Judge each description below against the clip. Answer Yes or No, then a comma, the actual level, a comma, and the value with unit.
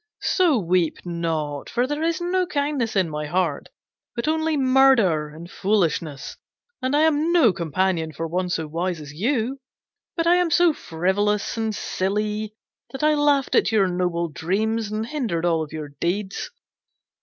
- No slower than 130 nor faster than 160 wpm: Yes, average, 155 wpm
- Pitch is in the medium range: No, high, 205 Hz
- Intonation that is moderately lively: No, wide, 8.4 semitones